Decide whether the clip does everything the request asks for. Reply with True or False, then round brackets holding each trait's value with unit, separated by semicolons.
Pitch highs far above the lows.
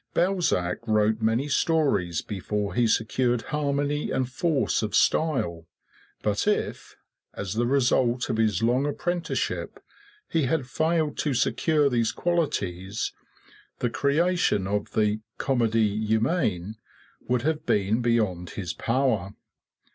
True (5.7 semitones)